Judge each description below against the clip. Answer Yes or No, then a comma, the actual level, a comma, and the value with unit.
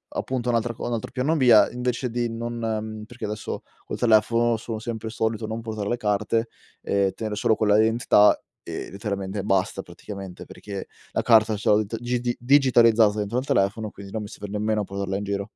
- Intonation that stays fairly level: Yes, narrow, 2.3 semitones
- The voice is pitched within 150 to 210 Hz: No, low, 110 Hz